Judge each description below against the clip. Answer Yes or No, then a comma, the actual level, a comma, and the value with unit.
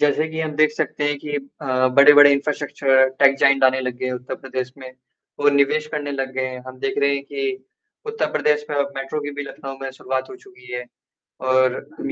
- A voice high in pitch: No, medium, 140 Hz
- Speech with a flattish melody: Yes, narrow, 2.2 semitones